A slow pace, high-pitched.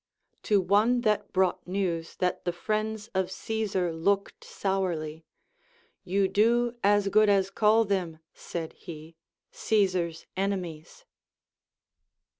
Yes: slow, 110 wpm; high, 195 Hz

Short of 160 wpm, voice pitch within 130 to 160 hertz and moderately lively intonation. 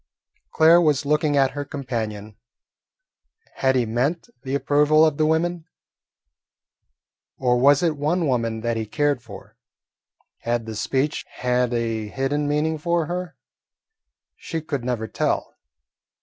Yes: slow, 135 wpm; medium, 140 Hz; average, 4.5 semitones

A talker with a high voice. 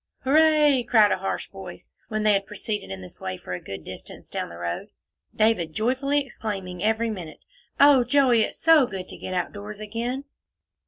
Yes: high, 215 Hz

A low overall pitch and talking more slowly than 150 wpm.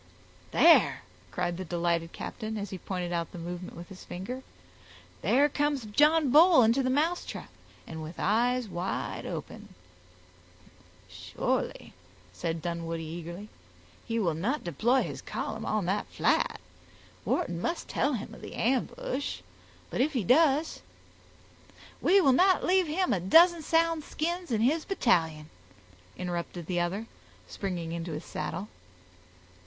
No: high, 215 Hz; average, 140 wpm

